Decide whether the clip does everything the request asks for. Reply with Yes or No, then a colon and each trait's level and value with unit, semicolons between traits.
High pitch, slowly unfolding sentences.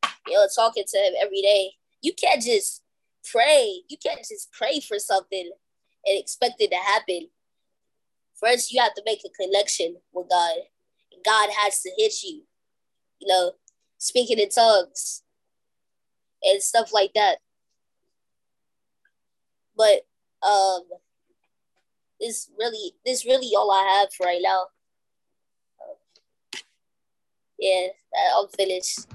Yes: high, 220 Hz; slow, 125 wpm